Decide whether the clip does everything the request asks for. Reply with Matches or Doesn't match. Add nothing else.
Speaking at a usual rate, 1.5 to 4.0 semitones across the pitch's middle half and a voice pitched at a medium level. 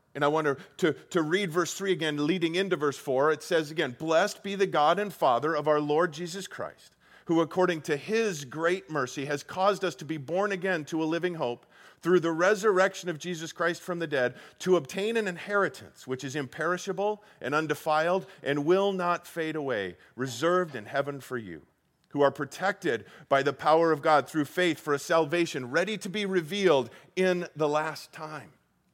Matches